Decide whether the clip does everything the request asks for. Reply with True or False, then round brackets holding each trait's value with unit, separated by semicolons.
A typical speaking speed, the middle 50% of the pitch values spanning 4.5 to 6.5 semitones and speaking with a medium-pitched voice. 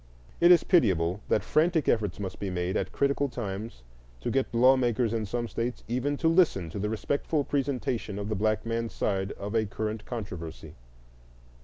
False (180 wpm; 4.9 semitones; 115 Hz)